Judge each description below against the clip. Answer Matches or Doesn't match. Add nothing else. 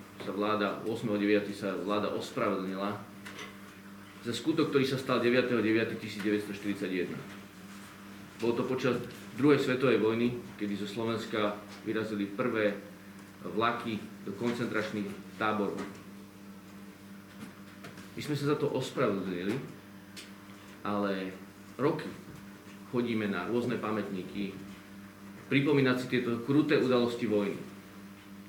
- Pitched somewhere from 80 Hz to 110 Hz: Matches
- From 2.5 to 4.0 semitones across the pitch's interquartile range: Matches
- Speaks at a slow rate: Matches